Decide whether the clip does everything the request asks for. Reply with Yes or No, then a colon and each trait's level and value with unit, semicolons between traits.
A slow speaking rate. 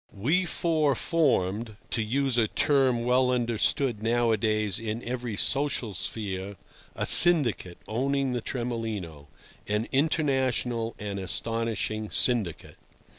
Yes: slow, 110 wpm